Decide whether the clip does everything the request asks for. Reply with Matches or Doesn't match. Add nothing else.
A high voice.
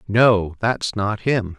Doesn't match